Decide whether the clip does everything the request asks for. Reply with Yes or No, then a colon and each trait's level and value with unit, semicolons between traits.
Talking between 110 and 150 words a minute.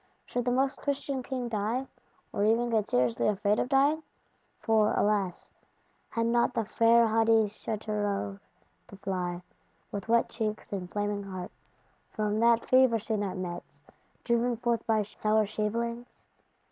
Yes: average, 145 wpm